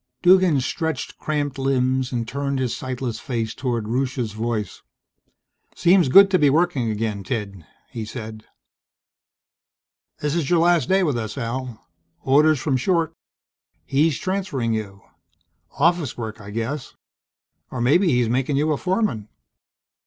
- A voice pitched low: Yes, low, 130 Hz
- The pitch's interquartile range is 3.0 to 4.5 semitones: No, average, 5.3 semitones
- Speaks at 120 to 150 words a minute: Yes, slow, 135 wpm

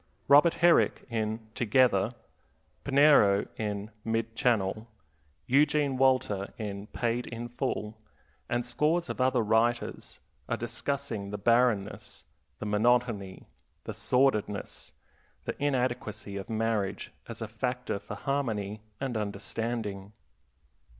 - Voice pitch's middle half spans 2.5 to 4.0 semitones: Yes, average, 3.6 semitones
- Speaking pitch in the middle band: No, low, 115 Hz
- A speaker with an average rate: No, slow, 110 wpm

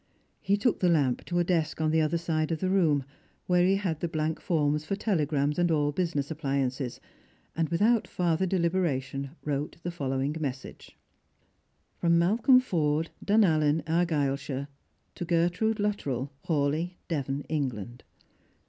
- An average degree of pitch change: Yes, average, 3.6 semitones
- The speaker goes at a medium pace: Yes, average, 150 wpm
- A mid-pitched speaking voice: Yes, medium, 160 Hz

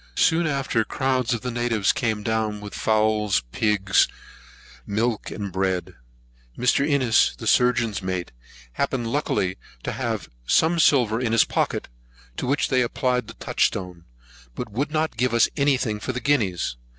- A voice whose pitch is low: Yes, low, 115 Hz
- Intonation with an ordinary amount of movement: Yes, average, 3.7 semitones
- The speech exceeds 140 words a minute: Yes, average, 150 wpm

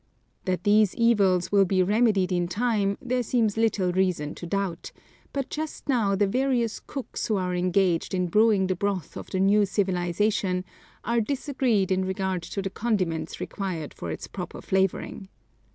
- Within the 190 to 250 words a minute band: No, average, 165 wpm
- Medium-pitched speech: No, high, 195 Hz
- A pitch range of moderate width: Yes, average, 3.2 semitones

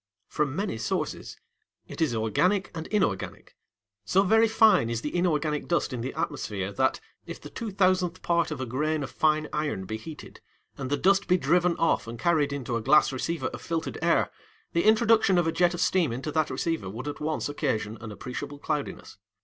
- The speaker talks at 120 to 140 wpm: No, average, 200 wpm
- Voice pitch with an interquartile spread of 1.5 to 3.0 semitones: No, wide, 5.6 semitones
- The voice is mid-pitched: Yes, medium, 155 Hz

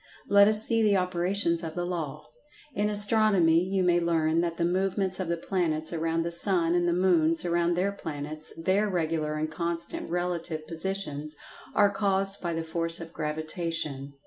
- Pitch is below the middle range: No, medium, 170 Hz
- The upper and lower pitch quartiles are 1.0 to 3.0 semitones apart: Yes, average, 2.7 semitones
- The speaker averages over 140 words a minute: Yes, average, 165 wpm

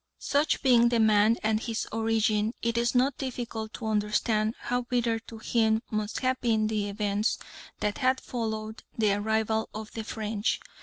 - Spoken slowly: No, average, 165 wpm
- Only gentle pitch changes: Yes, narrow, 1.7 semitones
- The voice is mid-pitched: No, high, 220 Hz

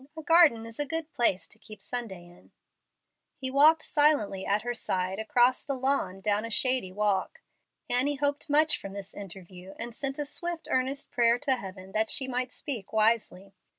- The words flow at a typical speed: Yes, average, 185 wpm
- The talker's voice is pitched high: Yes, high, 240 Hz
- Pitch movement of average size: No, wide, 6.2 semitones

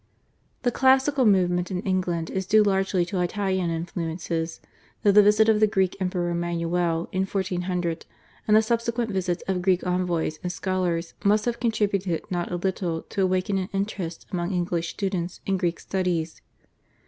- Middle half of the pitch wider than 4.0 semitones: No, narrow, 2.4 semitones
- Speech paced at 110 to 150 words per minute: No, average, 160 wpm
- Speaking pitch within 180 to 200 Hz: Yes, medium, 185 Hz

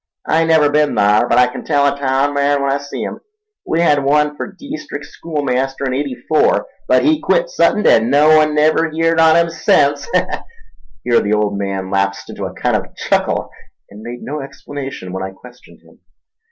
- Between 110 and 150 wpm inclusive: No, average, 195 wpm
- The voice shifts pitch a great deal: No, average, 4.4 semitones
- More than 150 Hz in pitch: No, medium, 145 Hz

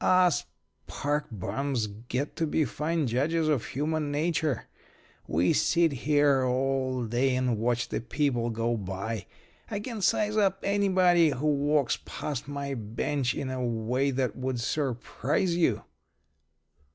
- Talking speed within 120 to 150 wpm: Yes, average, 140 wpm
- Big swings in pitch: No, average, 4.3 semitones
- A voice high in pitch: No, low, 135 Hz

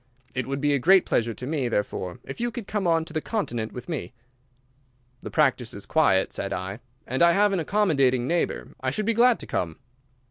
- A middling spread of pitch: No, wide, 8.2 semitones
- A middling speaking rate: No, fast, 215 wpm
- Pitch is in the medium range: Yes, medium, 145 Hz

